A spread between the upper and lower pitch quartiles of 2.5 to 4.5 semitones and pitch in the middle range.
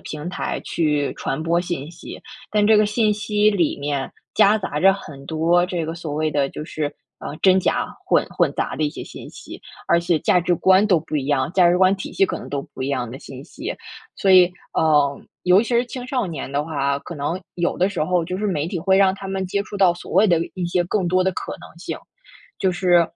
Yes: average, 4.0 semitones; medium, 175 Hz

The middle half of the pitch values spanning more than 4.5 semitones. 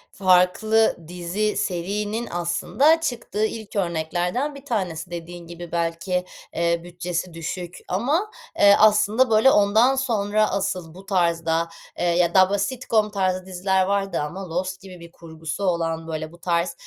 No: average, 3.6 semitones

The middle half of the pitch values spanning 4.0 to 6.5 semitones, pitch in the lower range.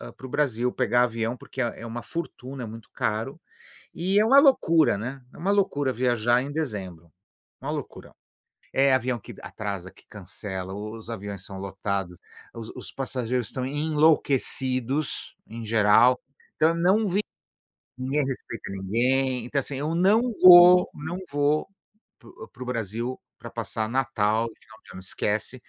Yes: average, 4.8 semitones; low, 125 Hz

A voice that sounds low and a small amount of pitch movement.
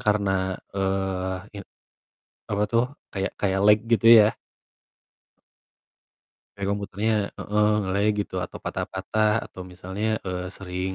Yes: low, 100 Hz; narrow, 1.9 semitones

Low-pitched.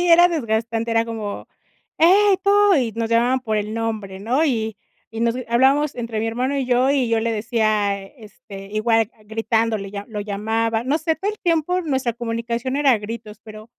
No: high, 230 Hz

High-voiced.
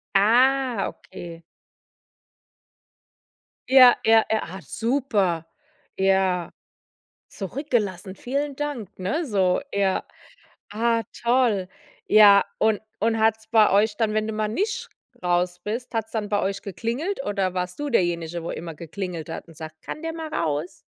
Yes: high, 210 Hz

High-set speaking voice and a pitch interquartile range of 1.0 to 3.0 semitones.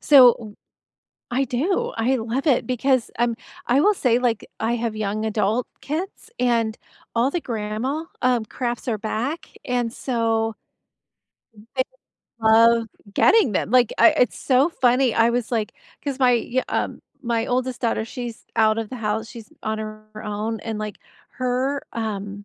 Yes: high, 235 Hz; narrow, 2.6 semitones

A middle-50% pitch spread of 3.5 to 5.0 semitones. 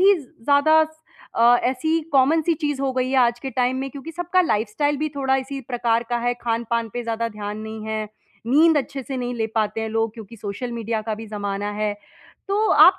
Yes: average, 4.2 semitones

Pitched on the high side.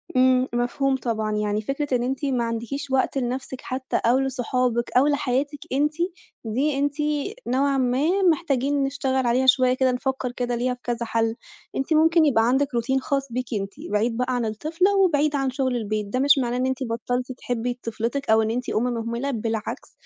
Yes: very high, 255 Hz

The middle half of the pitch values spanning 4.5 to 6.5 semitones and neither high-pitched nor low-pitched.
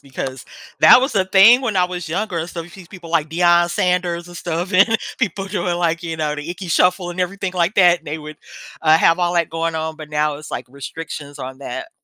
No: narrow, 2.4 semitones; medium, 175 Hz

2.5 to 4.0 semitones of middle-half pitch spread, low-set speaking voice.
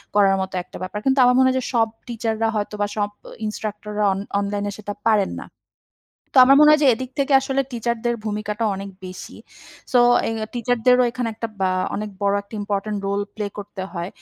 No: average, 3.1 semitones; high, 215 Hz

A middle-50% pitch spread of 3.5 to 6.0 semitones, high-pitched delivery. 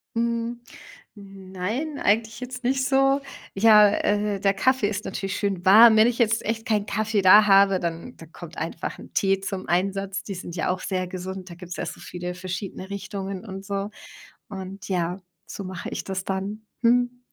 No: average, 3.0 semitones; high, 200 Hz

